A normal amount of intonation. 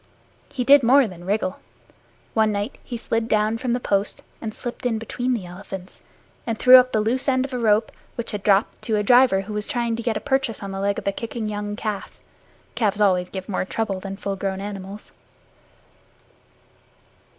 Yes: average, 3.3 semitones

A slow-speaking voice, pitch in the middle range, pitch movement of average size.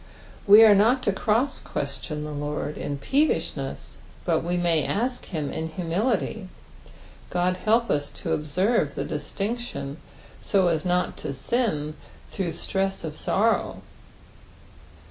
No: slow, 130 wpm; medium, 180 Hz; wide, 6.1 semitones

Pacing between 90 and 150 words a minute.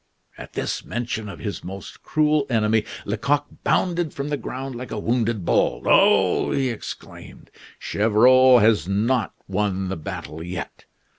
Yes: average, 145 wpm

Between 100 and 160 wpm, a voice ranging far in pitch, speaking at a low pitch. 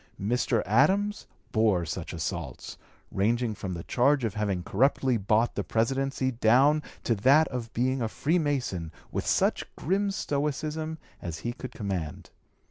Yes: average, 140 wpm; wide, 5.8 semitones; low, 120 Hz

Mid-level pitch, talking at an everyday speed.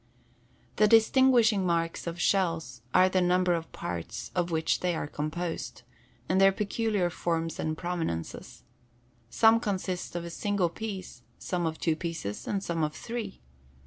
Yes: medium, 175 Hz; average, 150 wpm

